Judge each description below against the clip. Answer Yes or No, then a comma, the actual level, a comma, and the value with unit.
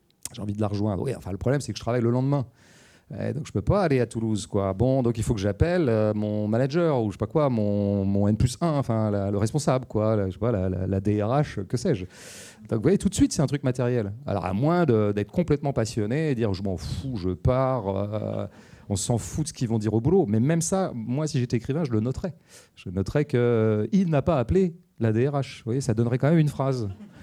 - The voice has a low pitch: Yes, low, 120 Hz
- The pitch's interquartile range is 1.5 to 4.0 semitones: No, average, 4.9 semitones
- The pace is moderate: No, fast, 260 wpm